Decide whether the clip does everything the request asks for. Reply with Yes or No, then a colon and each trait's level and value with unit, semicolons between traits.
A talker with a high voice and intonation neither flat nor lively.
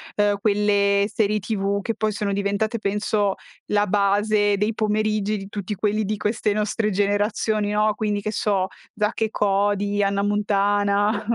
No: high, 205 Hz; narrow, 0.9 semitones